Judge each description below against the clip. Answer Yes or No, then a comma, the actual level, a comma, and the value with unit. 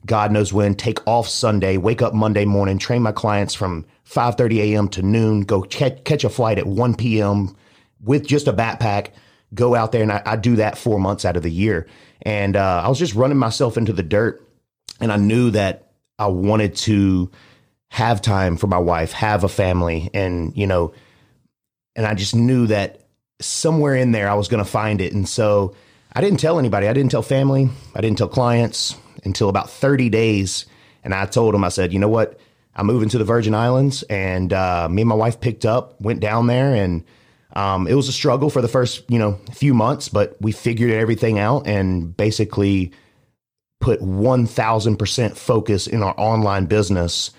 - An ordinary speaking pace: Yes, average, 195 wpm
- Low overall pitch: Yes, low, 110 Hz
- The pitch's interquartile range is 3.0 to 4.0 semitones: Yes, average, 3.3 semitones